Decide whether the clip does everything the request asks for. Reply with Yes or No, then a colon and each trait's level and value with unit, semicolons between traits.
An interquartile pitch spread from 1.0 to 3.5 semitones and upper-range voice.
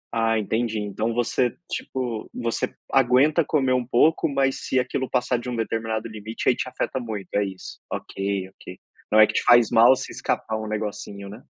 No: average, 2.9 semitones; low, 115 Hz